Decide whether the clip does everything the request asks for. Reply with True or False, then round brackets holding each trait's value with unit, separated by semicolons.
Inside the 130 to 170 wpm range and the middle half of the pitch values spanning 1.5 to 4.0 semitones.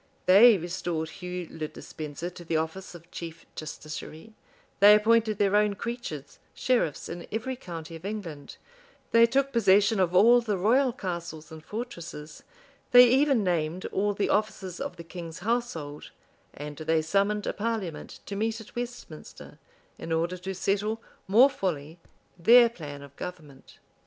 False (150 wpm; 5.4 semitones)